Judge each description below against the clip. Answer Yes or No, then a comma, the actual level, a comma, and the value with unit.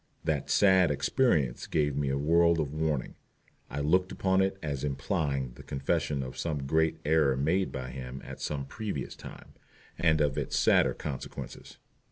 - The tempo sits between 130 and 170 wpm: Yes, average, 165 wpm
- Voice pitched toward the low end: Yes, very low, 75 Hz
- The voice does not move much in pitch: No, average, 3.5 semitones